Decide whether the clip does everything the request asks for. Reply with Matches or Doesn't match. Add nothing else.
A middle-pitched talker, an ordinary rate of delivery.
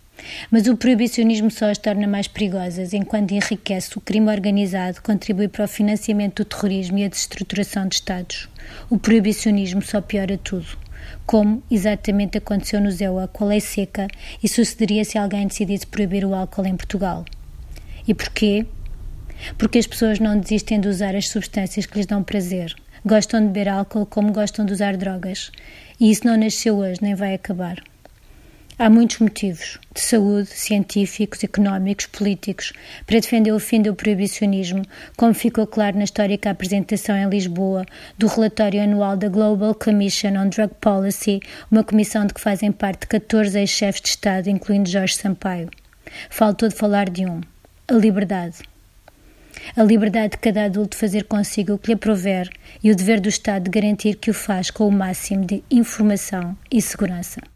Doesn't match